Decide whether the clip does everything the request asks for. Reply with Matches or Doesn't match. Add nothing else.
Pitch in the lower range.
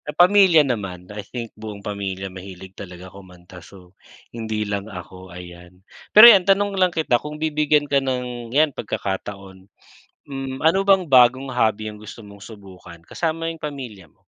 Matches